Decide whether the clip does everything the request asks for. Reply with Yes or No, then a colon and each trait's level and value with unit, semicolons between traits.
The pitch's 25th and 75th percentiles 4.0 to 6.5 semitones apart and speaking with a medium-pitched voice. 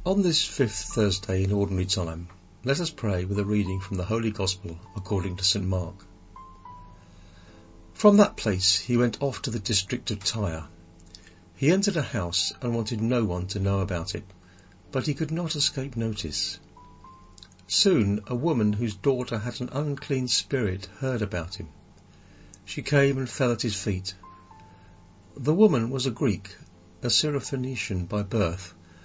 No: average, 5.2 semitones; low, 100 Hz